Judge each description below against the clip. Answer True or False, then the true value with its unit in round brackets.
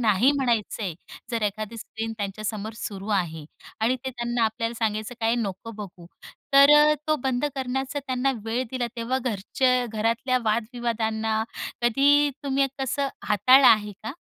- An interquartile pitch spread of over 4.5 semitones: False (3.2 semitones)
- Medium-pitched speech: False (230 Hz)